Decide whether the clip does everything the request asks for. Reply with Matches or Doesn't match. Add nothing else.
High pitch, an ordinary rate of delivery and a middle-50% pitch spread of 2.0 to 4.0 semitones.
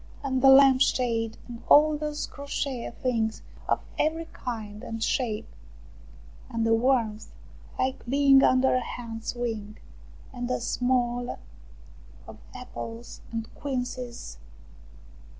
Doesn't match